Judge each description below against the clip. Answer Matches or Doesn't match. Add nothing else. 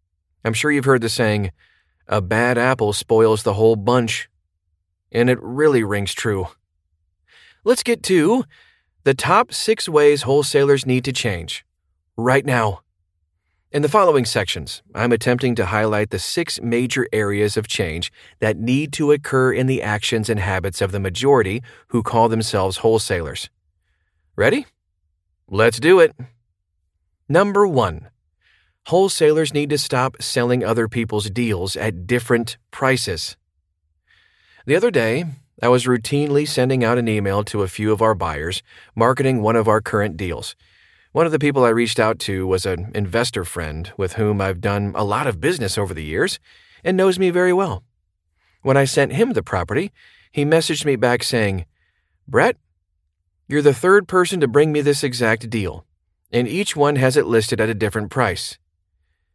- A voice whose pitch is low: Matches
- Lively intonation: Matches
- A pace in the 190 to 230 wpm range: Doesn't match